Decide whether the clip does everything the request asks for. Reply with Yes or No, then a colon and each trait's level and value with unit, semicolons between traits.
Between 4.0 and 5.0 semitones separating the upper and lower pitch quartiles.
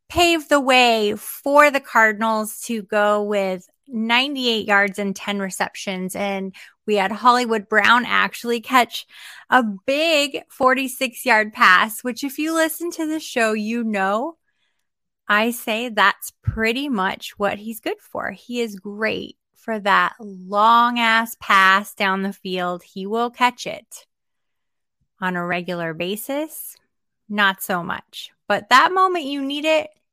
Yes: average, 4.5 semitones